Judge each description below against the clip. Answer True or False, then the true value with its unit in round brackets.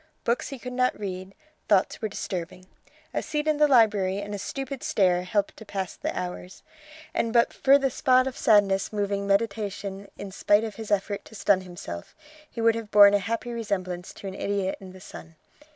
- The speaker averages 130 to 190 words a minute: False (200 wpm)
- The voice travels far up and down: False (3.2 semitones)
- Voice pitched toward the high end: True (205 Hz)